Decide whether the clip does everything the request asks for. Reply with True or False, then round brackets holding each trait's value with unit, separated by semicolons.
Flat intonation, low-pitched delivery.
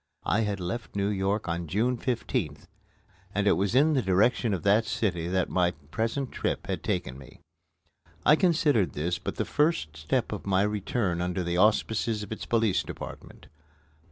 False (4.4 semitones; 100 Hz)